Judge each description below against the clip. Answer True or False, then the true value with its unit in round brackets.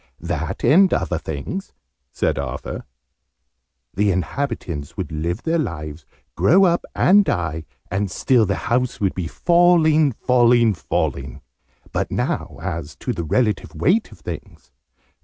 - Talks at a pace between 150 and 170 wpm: False (135 wpm)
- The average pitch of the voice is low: True (100 Hz)